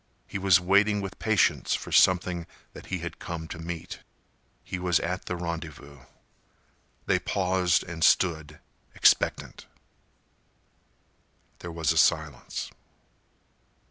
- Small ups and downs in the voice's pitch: Yes, narrow, 2.2 semitones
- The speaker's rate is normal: No, slow, 115 wpm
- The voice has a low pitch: Yes, very low, 85 Hz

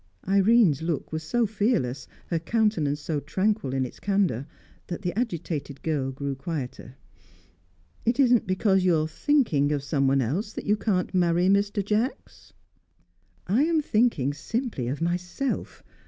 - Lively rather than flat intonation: Yes, wide, 6.8 semitones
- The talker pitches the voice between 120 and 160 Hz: No, medium, 175 Hz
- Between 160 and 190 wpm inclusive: No, average, 145 wpm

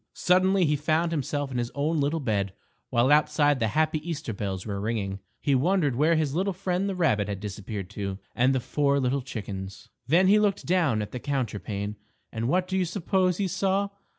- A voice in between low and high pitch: Yes, medium, 145 Hz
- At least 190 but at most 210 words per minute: Yes, fast, 205 wpm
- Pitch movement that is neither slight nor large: No, wide, 8.2 semitones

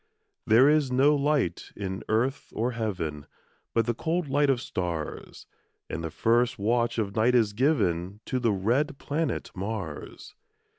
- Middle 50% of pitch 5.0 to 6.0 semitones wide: Yes, wide, 5.4 semitones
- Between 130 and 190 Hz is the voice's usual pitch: No, low, 115 Hz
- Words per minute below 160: Yes, average, 150 wpm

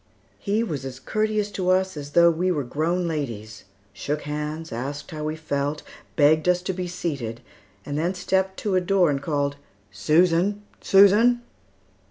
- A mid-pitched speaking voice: Yes, medium, 160 Hz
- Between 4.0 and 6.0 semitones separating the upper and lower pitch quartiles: Yes, average, 4.6 semitones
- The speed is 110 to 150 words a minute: No, average, 165 wpm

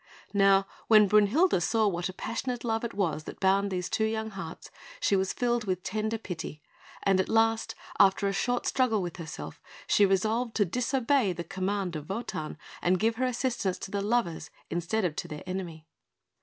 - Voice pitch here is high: Yes, high, 200 Hz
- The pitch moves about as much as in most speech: Yes, average, 3.6 semitones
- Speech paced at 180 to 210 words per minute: Yes, average, 185 wpm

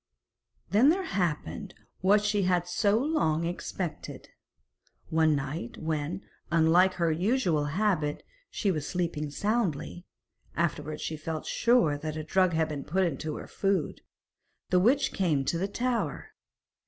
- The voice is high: No, medium, 170 Hz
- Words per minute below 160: Yes, average, 140 wpm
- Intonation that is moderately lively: Yes, average, 4.4 semitones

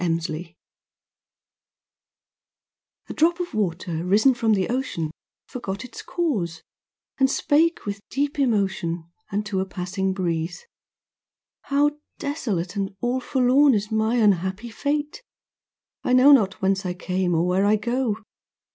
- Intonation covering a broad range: Yes, wide, 6.0 semitones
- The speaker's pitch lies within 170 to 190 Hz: No, high, 205 Hz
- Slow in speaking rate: Yes, slow, 130 wpm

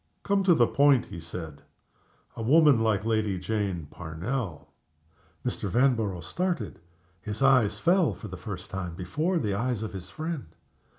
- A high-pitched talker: No, low, 110 Hz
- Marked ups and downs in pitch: Yes, wide, 6.6 semitones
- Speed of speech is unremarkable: Yes, average, 160 wpm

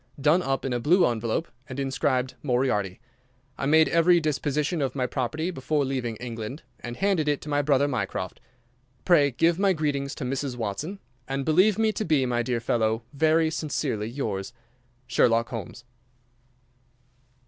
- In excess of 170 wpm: No, average, 160 wpm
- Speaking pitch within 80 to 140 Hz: Yes, low, 135 Hz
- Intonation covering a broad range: No, average, 4.4 semitones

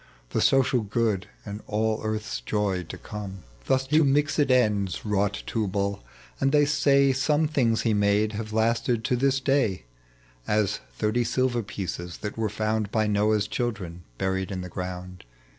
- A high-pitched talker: No, low, 110 Hz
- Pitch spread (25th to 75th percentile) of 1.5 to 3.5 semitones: No, average, 4.1 semitones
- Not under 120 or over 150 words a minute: No, average, 160 wpm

